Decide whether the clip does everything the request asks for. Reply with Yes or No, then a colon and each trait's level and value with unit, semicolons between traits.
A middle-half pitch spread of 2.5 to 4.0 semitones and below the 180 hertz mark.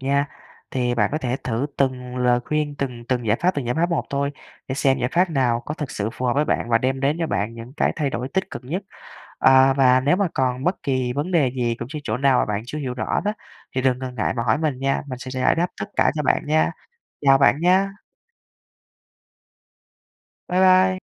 Yes: average, 3.5 semitones; low, 135 Hz